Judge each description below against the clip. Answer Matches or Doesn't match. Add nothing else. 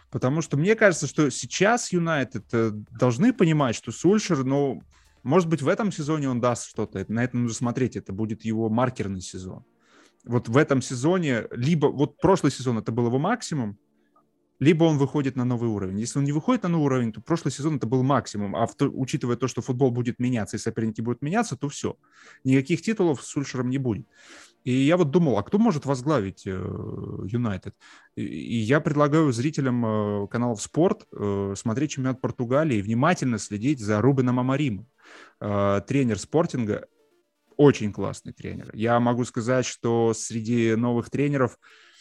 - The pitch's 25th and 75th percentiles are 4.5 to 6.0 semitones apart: Matches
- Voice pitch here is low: Matches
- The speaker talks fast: Matches